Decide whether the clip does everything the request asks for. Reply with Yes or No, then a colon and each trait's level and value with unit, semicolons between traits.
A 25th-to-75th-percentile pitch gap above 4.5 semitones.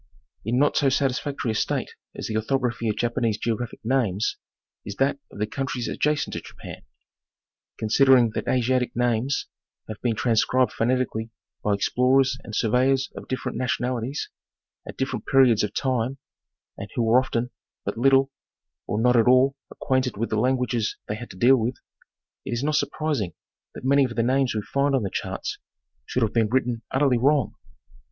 No: average, 2.9 semitones